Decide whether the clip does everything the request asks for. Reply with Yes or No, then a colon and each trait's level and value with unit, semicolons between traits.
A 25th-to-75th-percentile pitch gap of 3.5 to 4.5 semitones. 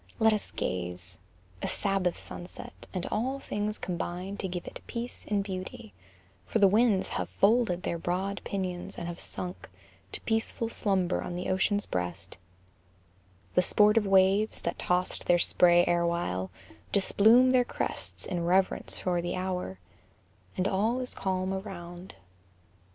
No: average, 2.9 semitones